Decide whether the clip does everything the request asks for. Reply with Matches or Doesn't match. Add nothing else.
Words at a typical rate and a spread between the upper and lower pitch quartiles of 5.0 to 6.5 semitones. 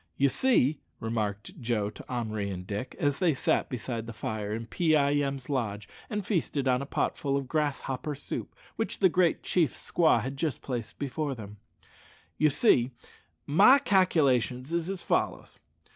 Matches